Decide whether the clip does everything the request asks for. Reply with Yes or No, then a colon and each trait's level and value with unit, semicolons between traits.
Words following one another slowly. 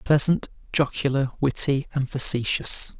Yes: slow, 100 wpm